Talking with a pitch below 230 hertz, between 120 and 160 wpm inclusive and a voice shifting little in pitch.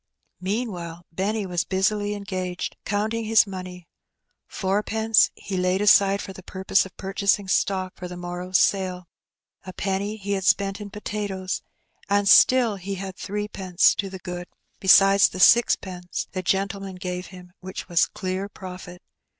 Yes: high, 190 Hz; average, 150 wpm; narrow, 1.7 semitones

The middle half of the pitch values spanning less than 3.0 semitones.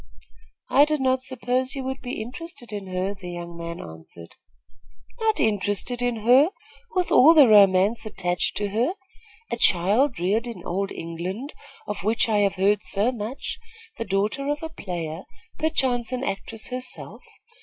No: average, 5.2 semitones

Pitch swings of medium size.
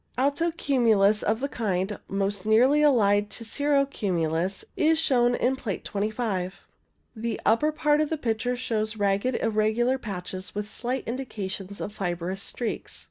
Yes: average, 4.5 semitones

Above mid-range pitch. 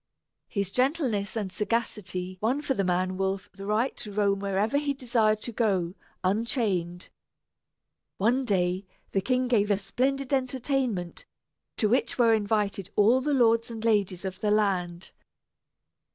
Yes: high, 210 Hz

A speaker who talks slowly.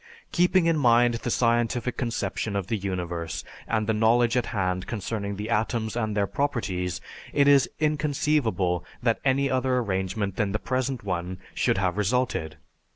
No: average, 155 wpm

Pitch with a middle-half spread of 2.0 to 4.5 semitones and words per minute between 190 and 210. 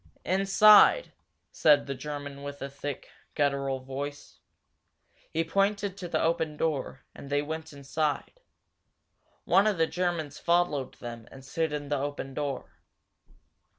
No: average, 3.4 semitones; slow, 135 wpm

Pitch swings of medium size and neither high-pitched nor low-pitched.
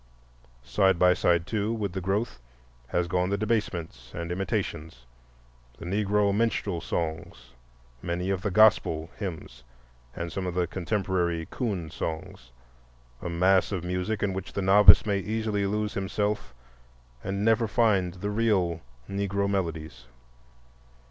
No: average, 3.6 semitones; very low, 95 Hz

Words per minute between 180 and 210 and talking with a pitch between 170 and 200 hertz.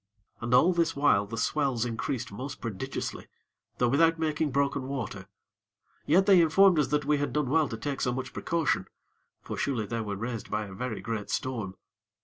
No: average, 185 wpm; low, 130 Hz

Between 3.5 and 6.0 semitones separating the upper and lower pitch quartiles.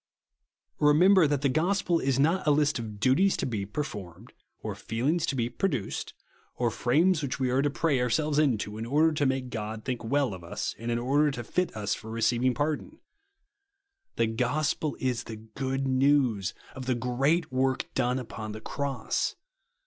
Yes: average, 4.1 semitones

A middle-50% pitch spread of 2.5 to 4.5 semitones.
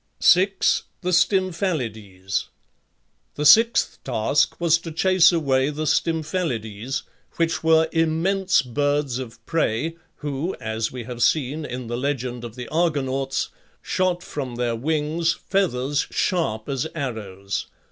No: average, 5.3 semitones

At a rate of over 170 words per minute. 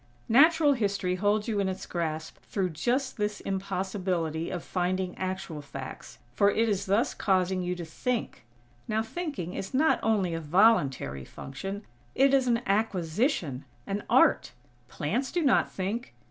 No: average, 150 wpm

